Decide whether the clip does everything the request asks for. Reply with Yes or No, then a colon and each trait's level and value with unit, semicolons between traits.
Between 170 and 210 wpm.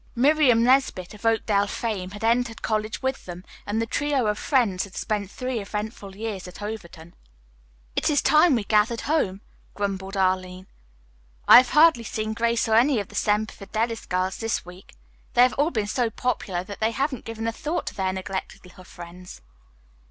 Yes: average, 180 wpm